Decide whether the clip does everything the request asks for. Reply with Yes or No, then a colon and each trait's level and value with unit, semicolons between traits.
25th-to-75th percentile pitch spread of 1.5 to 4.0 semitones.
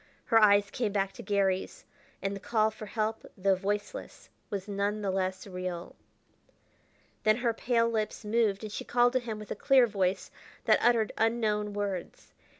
Yes: narrow, 2.4 semitones